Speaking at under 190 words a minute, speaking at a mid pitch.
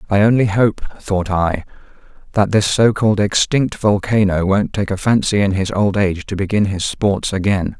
No: average, 175 wpm; low, 100 Hz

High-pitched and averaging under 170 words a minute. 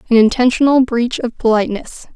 Yes: high, 240 Hz; average, 140 wpm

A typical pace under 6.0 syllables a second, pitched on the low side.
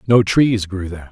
Yes: 5.3 syllables/s; low, 100 Hz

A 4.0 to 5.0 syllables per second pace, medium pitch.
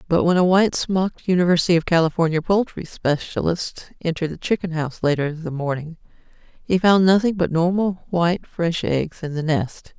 No: 5.6 syllables/s; medium, 170 Hz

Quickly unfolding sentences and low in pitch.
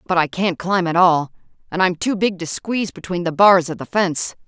No: fast, 240 wpm; medium, 175 Hz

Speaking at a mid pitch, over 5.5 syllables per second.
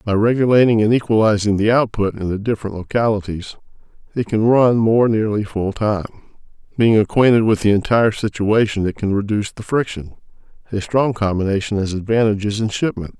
No: low, 105 Hz; 5.7 syllables/s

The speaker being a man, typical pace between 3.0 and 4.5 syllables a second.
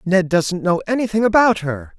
No: male; 5.0 syllables/s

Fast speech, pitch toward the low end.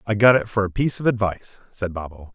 Yes: fast, 255 wpm; low, 105 Hz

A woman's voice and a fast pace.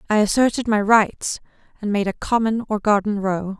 No: female; average, 185 wpm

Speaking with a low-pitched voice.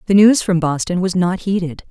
No: medium, 185 Hz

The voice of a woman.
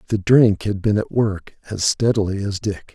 No: male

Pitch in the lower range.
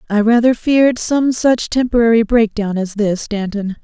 No: high, 225 Hz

